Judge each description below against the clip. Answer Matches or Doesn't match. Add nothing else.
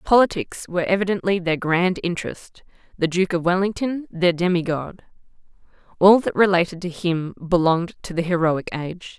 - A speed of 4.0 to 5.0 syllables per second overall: Doesn't match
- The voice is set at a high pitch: Doesn't match